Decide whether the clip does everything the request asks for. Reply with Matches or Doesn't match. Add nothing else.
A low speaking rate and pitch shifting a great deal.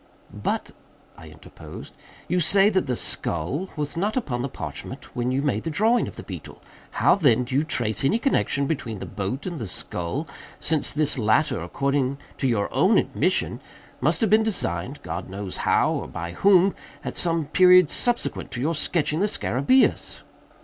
Doesn't match